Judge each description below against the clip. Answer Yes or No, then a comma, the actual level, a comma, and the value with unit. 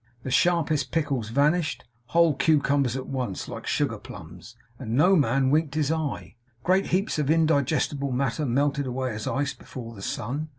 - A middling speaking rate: Yes, average, 165 wpm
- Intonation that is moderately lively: Yes, average, 3.3 semitones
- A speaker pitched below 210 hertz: Yes, medium, 140 Hz